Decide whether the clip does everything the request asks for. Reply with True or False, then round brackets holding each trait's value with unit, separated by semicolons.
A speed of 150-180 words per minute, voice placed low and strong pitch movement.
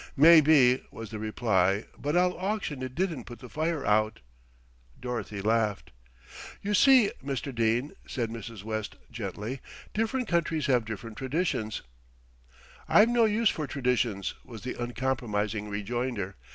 False (140 wpm; 125 Hz; 6.2 semitones)